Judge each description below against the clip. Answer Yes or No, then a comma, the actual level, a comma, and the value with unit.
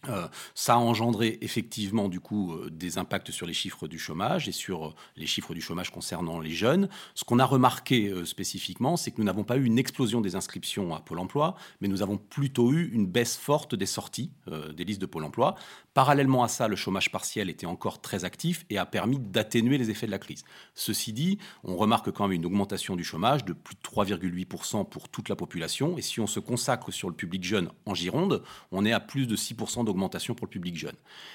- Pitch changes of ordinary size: Yes, average, 4.7 semitones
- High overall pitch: No, low, 110 Hz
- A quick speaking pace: Yes, fast, 230 wpm